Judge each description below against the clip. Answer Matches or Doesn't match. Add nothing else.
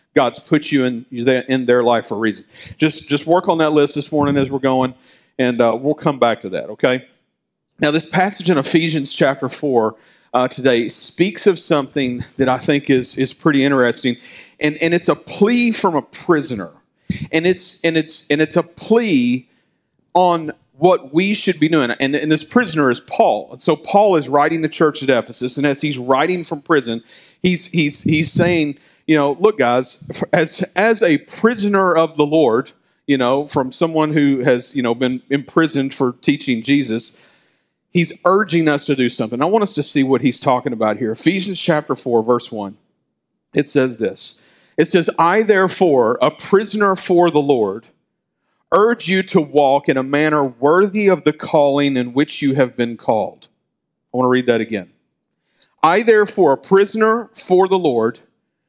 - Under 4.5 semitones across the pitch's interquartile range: Doesn't match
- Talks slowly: Doesn't match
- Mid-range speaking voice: Matches